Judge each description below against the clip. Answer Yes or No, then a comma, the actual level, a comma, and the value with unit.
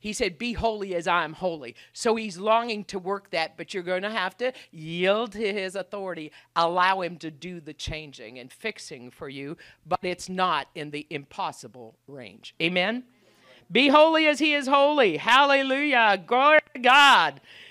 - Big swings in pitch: Yes, wide, 5.8 semitones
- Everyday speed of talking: Yes, average, 175 wpm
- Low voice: No, high, 190 Hz